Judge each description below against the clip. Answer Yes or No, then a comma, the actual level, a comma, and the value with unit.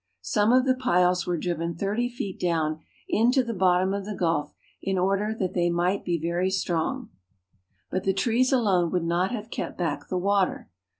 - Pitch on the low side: No, medium, 185 Hz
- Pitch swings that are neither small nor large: Yes, average, 3.4 semitones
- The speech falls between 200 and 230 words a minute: No, average, 185 wpm